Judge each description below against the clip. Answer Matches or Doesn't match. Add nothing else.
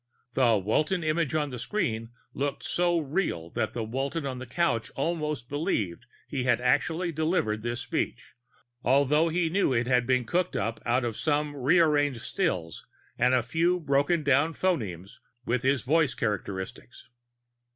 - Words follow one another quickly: Doesn't match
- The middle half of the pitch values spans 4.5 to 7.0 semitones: Matches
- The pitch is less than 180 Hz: Matches